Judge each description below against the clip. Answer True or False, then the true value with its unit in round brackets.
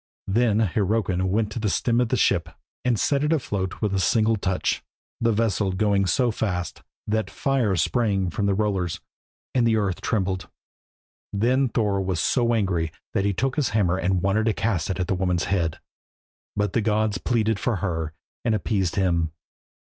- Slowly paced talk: False (180 wpm)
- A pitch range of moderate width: True (3.3 semitones)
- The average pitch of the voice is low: True (105 Hz)